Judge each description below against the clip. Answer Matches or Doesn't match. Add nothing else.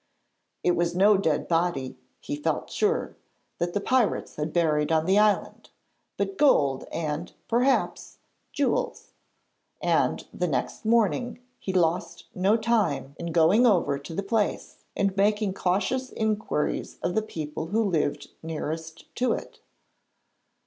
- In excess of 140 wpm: Doesn't match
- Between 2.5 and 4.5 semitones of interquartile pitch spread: Doesn't match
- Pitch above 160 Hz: Matches